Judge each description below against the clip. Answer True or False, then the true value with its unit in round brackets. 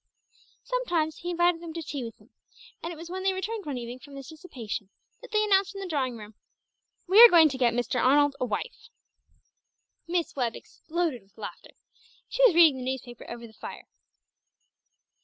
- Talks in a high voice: True (310 Hz)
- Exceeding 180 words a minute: True (190 wpm)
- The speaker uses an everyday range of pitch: False (6.2 semitones)